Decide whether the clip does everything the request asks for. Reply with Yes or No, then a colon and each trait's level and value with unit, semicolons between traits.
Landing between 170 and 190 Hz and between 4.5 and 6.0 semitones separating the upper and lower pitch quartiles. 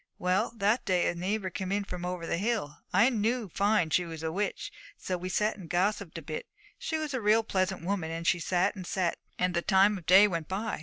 No: medium, 185 Hz; average, 3.0 semitones